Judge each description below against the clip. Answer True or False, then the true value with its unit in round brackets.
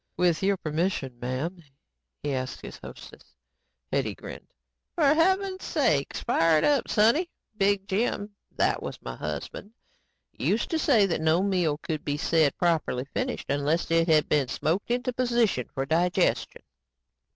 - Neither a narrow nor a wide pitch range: False (7.1 semitones)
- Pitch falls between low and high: True (175 Hz)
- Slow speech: False (150 wpm)